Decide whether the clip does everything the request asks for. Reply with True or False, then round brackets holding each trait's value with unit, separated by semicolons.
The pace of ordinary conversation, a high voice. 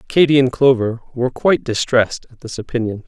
False (175 wpm; 125 Hz)